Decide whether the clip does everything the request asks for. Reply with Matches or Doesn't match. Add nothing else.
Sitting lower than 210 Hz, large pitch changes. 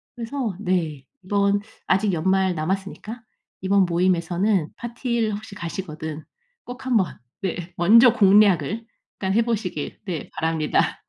Doesn't match